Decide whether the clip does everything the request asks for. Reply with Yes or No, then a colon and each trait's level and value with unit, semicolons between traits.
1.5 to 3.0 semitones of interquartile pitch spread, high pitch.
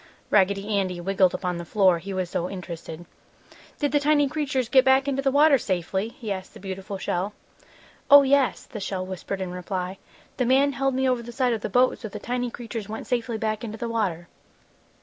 No: wide, 5.5 semitones; high, 215 Hz